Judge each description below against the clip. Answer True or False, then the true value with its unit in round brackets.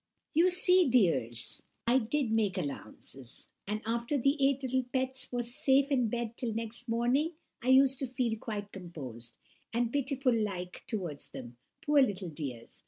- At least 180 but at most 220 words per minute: False (165 wpm)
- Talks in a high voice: True (235 Hz)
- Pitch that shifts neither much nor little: False (5.7 semitones)